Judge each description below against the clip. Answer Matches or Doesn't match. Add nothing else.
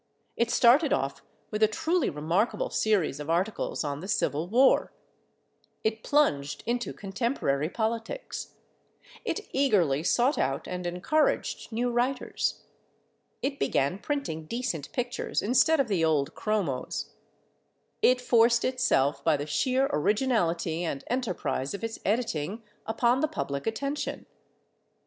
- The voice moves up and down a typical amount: Doesn't match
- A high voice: Matches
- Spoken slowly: Matches